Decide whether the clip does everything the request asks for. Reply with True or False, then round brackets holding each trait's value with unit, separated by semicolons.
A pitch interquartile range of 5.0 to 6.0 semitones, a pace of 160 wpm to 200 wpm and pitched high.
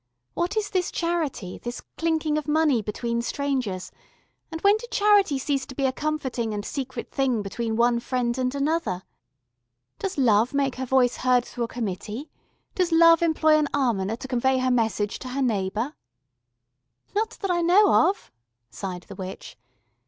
True (5.3 semitones; 165 wpm; 260 Hz)